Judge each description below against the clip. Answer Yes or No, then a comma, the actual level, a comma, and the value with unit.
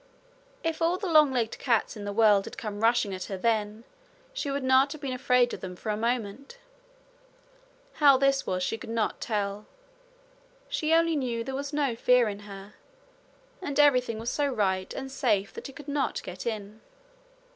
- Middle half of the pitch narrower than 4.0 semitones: No, average, 4.9 semitones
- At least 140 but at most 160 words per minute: No, average, 190 wpm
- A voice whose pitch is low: No, high, 240 Hz